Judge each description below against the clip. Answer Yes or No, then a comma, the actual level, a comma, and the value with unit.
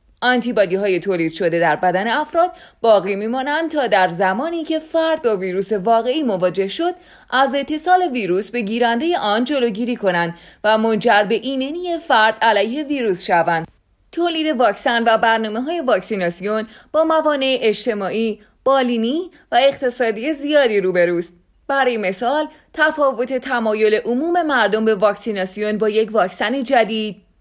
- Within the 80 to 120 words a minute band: No, average, 135 wpm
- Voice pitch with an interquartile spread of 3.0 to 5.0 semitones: No, wide, 5.4 semitones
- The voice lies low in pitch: No, high, 230 Hz